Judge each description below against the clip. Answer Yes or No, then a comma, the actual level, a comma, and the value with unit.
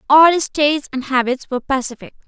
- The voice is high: Yes, very high, 275 Hz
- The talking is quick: No, average, 185 wpm